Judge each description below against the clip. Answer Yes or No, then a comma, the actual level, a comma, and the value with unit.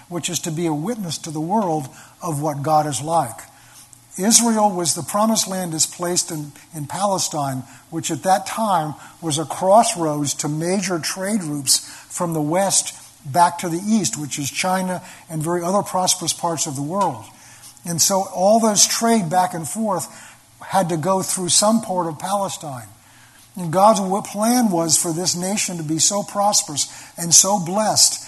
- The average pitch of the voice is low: No, medium, 175 Hz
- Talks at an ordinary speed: Yes, average, 175 wpm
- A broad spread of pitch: No, average, 3.9 semitones